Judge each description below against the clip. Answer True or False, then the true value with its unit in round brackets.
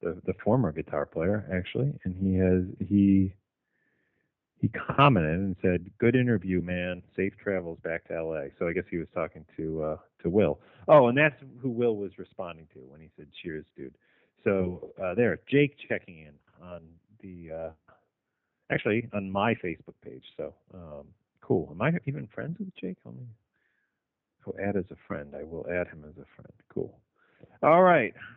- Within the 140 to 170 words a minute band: False (180 wpm)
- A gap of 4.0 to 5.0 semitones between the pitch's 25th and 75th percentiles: True (4.4 semitones)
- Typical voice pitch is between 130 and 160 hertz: False (95 Hz)